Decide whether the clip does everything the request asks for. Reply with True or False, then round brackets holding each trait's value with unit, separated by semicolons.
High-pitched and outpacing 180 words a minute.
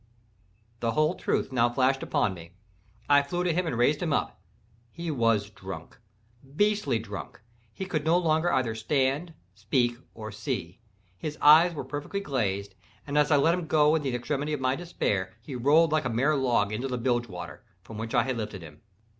False (130 Hz; 190 wpm)